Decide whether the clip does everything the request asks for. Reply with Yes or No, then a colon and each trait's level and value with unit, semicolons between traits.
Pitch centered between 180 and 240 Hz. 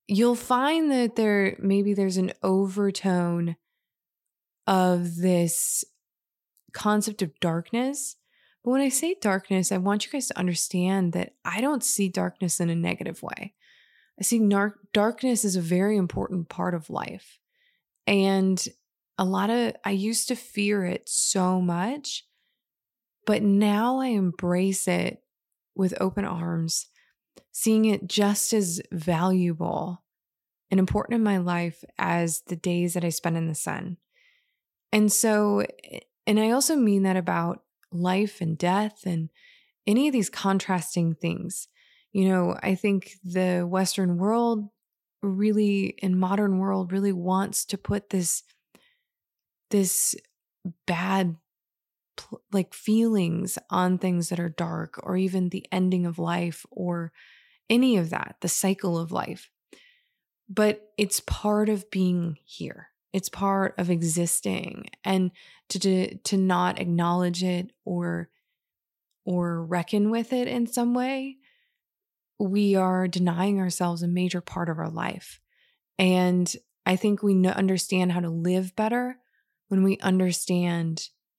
Yes: high, 190 Hz